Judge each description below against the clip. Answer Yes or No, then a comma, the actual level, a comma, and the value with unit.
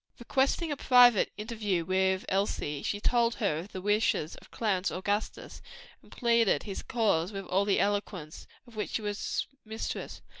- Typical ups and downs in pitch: Yes, average, 3.3 semitones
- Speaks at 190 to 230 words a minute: No, average, 160 wpm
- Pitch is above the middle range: Yes, high, 205 Hz